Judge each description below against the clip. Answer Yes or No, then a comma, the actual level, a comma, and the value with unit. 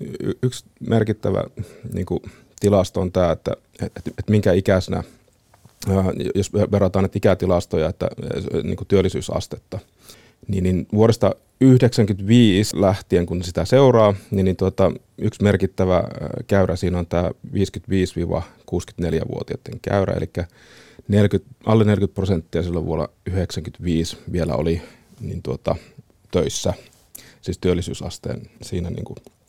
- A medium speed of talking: Yes, average, 110 wpm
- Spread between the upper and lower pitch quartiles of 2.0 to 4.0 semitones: Yes, average, 3.3 semitones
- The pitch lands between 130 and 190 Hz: No, low, 100 Hz